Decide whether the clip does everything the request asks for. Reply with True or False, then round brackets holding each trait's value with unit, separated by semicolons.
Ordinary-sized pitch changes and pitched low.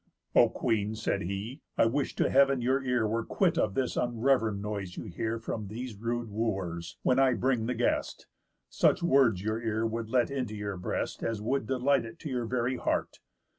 True (3.2 semitones; 115 Hz)